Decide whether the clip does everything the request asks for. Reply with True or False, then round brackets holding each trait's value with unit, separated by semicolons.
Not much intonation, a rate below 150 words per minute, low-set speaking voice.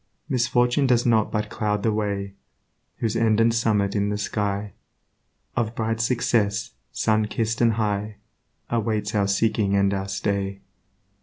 True (2.0 semitones; 135 wpm; 105 Hz)